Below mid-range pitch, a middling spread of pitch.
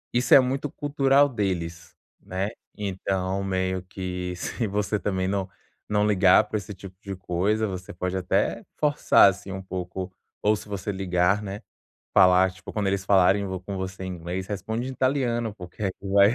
No: very low, 95 Hz; narrow, 2.2 semitones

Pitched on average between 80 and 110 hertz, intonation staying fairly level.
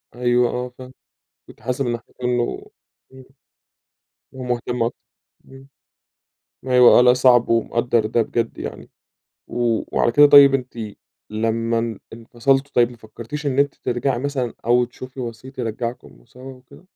No: low, 125 Hz; narrow, 1.8 semitones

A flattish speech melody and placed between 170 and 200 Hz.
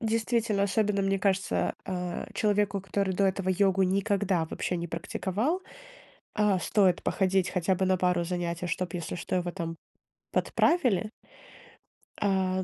Yes: narrow, 2.0 semitones; high, 190 Hz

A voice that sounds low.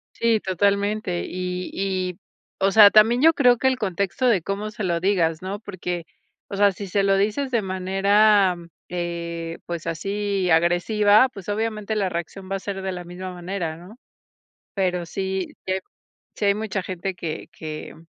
No: high, 195 Hz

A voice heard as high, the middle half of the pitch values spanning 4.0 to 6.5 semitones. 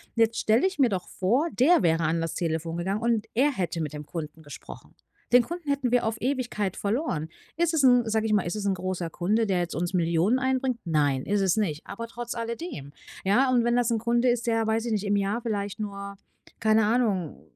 Yes: high, 215 Hz; average, 5.2 semitones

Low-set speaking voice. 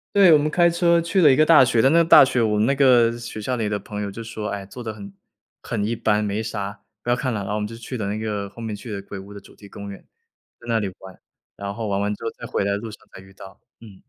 Yes: low, 110 Hz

